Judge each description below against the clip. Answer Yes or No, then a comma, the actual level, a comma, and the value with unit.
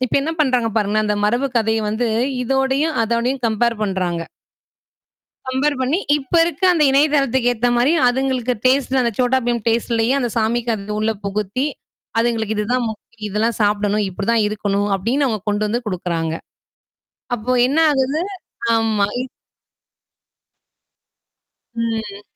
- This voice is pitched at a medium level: No, high, 230 Hz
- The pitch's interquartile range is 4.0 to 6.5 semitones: No, average, 3.5 semitones